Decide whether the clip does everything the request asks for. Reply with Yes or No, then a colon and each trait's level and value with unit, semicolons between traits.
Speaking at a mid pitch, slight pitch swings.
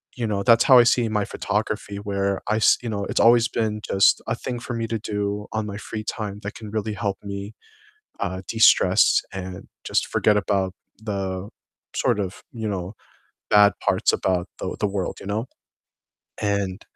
No: low, 105 Hz; narrow, 1.8 semitones